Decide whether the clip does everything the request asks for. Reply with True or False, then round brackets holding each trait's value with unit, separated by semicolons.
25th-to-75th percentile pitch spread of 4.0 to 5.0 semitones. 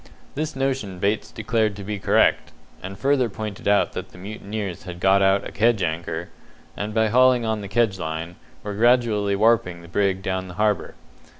False (2.9 semitones)